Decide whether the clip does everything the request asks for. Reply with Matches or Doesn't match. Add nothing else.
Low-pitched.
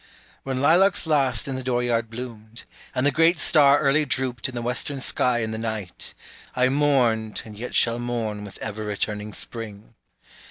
Matches